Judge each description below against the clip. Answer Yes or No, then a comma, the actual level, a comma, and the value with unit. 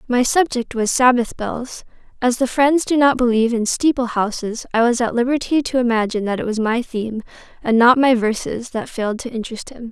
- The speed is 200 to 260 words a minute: Yes, fast, 205 wpm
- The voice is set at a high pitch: Yes, high, 240 Hz